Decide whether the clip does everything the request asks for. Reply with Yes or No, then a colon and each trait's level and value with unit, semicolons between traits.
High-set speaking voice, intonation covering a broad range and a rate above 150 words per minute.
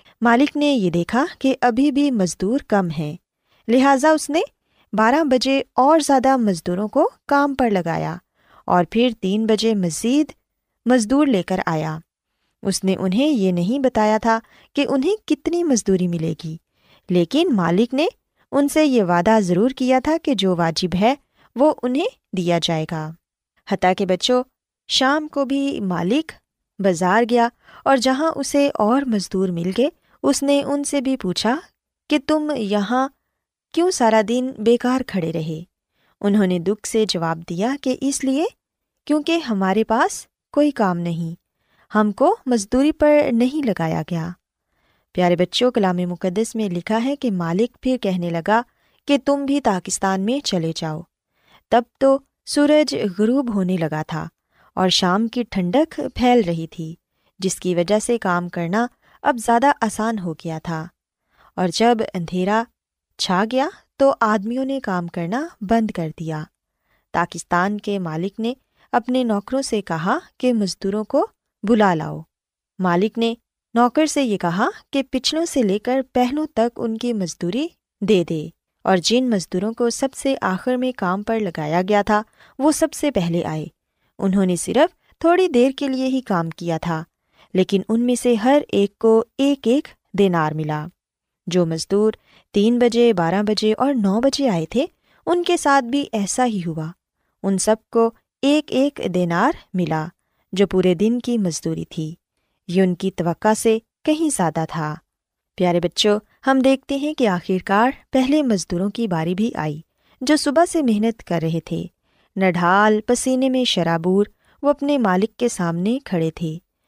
Yes: high, 220 Hz; wide, 6.7 semitones; average, 160 wpm